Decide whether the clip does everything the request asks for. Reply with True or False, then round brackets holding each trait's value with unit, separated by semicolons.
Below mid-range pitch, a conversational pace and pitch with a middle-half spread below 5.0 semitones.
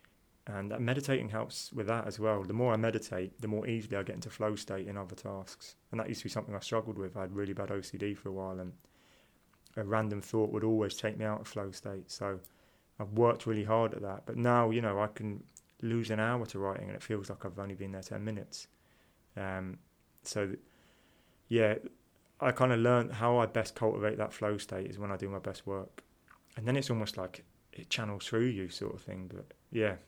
False (105 Hz; 230 wpm; 2.5 semitones)